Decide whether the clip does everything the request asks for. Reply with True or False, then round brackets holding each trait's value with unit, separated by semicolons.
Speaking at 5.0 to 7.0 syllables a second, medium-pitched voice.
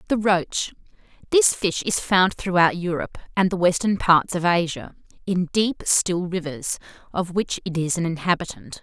False (4.7 syllables/s; 180 Hz)